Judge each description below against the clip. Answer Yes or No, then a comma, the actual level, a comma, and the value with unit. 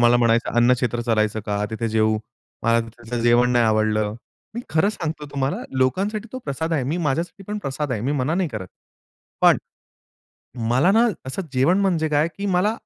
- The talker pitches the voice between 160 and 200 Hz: No, low, 130 Hz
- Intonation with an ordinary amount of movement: No, wide, 6.2 semitones